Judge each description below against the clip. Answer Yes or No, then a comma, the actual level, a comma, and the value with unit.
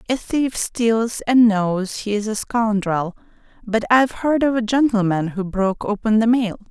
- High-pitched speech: Yes, high, 220 Hz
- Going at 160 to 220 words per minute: Yes, average, 180 wpm